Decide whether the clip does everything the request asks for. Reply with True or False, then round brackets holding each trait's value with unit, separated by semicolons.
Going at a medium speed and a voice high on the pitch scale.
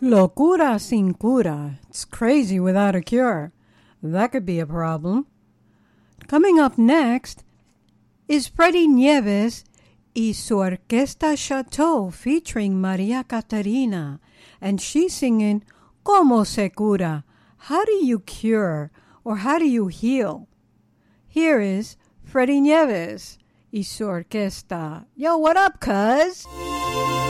False (110 wpm; 225 Hz)